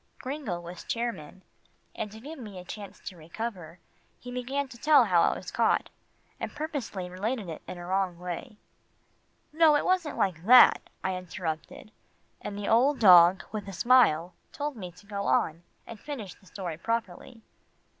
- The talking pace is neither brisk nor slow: Yes, average, 170 wpm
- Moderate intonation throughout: No, wide, 5.7 semitones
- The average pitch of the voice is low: No, high, 200 Hz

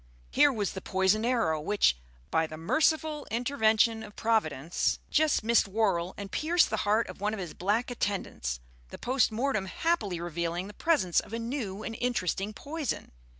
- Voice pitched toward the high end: Yes, high, 215 Hz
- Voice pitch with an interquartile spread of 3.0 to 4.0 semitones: No, average, 4.7 semitones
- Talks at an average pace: Yes, average, 170 wpm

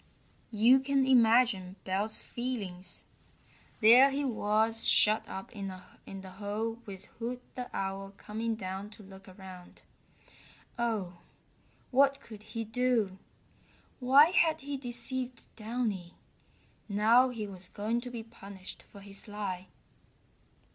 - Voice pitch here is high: Yes, high, 220 Hz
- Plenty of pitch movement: No, average, 4.1 semitones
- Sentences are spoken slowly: Yes, slow, 120 wpm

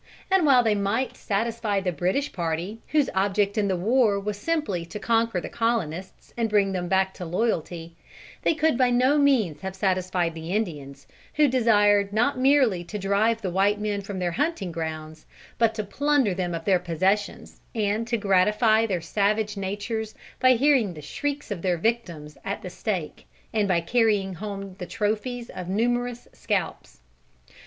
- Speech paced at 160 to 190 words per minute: Yes, average, 175 wpm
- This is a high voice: Yes, high, 205 Hz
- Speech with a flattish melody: No, average, 4.1 semitones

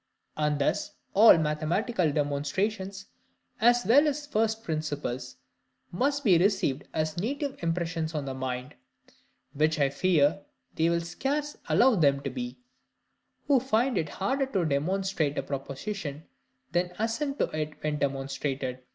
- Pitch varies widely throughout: Yes, wide, 7.3 semitones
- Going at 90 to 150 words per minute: Yes, slow, 135 wpm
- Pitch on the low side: No, medium, 170 Hz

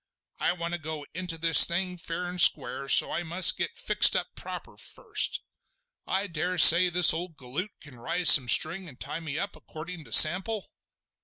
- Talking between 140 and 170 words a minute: No, average, 185 wpm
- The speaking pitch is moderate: Yes, medium, 170 Hz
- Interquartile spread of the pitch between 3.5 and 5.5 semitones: No, average, 2.7 semitones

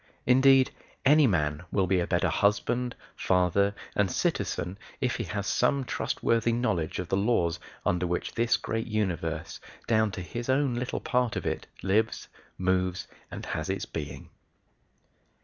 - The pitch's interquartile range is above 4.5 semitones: Yes, average, 5.1 semitones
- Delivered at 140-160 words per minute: Yes, average, 150 wpm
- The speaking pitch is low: Yes, low, 105 Hz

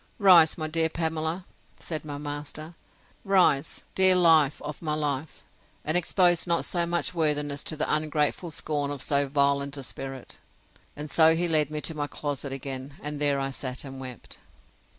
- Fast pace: No, average, 170 wpm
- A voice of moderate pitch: Yes, medium, 150 Hz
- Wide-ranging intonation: No, narrow, 2.5 semitones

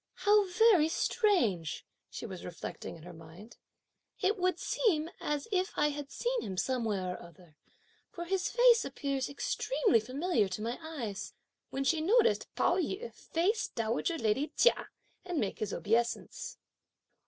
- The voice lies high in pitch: Yes, very high, 295 Hz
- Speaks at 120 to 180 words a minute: Yes, average, 150 wpm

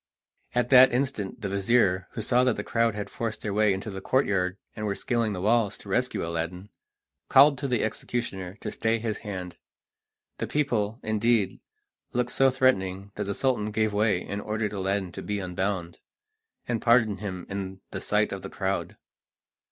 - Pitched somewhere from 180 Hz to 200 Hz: No, low, 105 Hz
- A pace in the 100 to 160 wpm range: No, average, 180 wpm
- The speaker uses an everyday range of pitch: Yes, average, 3.6 semitones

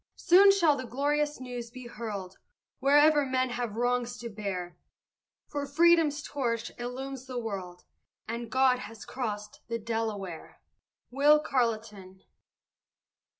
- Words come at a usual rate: No, slow, 120 wpm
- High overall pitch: Yes, high, 245 Hz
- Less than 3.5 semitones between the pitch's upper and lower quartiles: No, average, 4.0 semitones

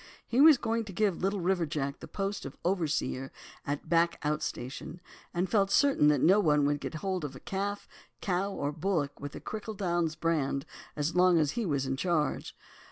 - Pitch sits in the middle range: Yes, medium, 170 Hz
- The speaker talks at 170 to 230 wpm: Yes, average, 195 wpm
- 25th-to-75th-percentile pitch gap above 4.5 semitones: Yes, average, 4.9 semitones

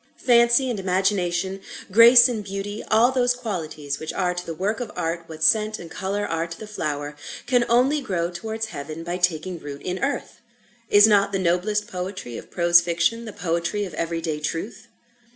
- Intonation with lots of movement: No, average, 4.5 semitones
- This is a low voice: No, high, 190 Hz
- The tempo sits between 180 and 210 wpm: Yes, average, 190 wpm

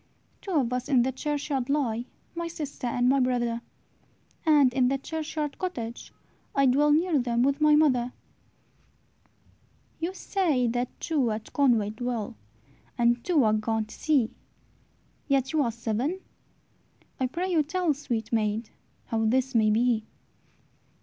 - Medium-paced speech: Yes, average, 145 wpm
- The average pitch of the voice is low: No, very high, 255 Hz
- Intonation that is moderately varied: Yes, average, 4.1 semitones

